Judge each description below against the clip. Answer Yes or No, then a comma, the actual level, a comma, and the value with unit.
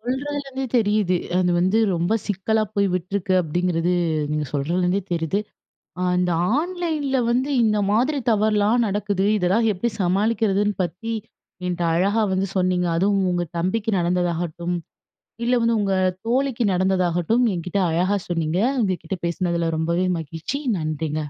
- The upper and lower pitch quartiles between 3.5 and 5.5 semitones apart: Yes, average, 4.0 semitones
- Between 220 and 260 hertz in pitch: No, high, 190 Hz